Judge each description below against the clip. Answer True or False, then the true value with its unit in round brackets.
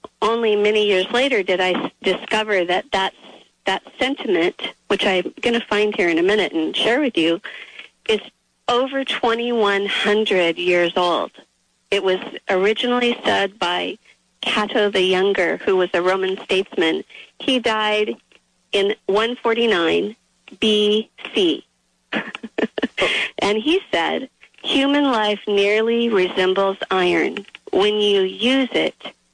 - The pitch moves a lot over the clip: False (4.1 semitones)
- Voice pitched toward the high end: True (210 Hz)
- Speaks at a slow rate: True (120 wpm)